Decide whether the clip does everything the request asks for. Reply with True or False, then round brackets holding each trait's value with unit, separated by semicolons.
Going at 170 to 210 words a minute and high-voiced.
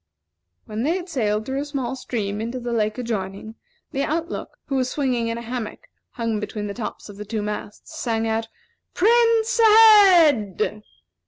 True (175 wpm; 240 Hz)